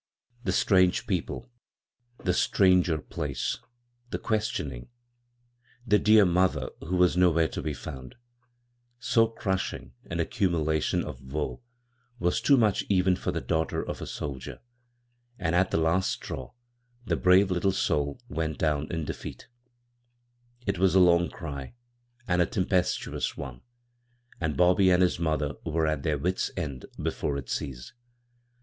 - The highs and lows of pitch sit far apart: No, average, 3.6 semitones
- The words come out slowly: No, average, 145 wpm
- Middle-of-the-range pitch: No, very low, 90 Hz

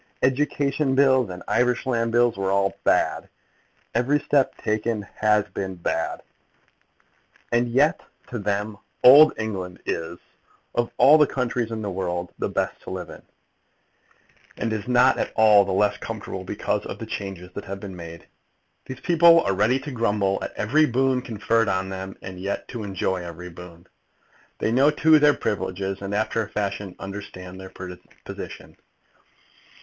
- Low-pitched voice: Yes, low, 105 Hz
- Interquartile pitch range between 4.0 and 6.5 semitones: Yes, average, 4.7 semitones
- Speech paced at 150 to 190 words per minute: Yes, average, 160 wpm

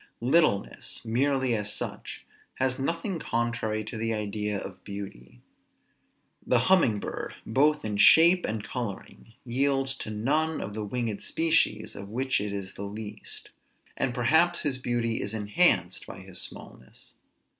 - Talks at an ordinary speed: Yes, average, 145 wpm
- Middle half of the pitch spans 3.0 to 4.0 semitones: No, average, 4.6 semitones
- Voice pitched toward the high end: No, low, 115 Hz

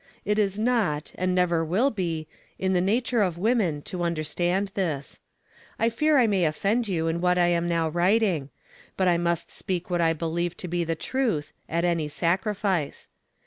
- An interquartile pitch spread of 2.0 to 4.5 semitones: Yes, average, 3.4 semitones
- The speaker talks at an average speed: Yes, average, 185 wpm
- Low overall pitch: No, medium, 175 Hz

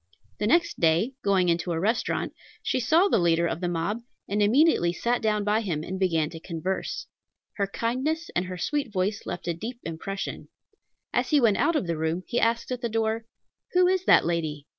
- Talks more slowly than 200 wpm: No, fast, 205 wpm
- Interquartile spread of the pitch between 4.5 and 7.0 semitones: Yes, wide, 5.6 semitones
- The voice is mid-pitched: No, high, 200 Hz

